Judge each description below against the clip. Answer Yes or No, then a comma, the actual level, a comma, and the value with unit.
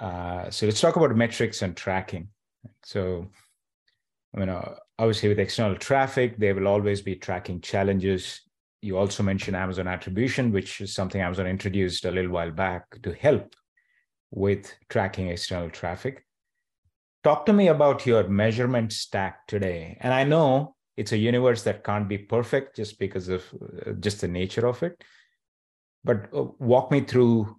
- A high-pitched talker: No, low, 100 Hz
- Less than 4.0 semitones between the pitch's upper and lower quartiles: No, average, 4.4 semitones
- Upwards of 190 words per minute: No, average, 160 wpm